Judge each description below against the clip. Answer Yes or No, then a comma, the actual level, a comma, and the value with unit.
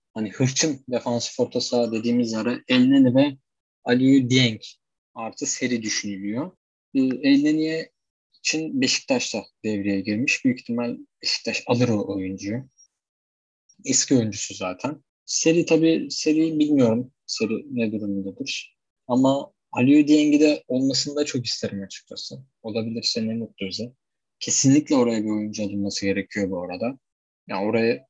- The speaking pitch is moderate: No, low, 125 Hz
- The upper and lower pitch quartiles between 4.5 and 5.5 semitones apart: No, average, 4.1 semitones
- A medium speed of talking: Yes, average, 125 wpm